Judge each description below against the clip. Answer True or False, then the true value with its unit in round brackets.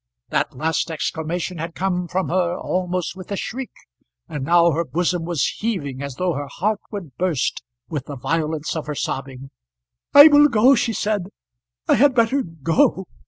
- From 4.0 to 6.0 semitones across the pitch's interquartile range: True (4.4 semitones)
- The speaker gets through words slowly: False (170 wpm)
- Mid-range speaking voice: True (175 Hz)